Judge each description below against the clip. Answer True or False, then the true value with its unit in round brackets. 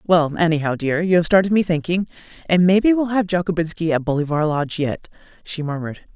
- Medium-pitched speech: True (170 Hz)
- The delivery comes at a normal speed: True (185 wpm)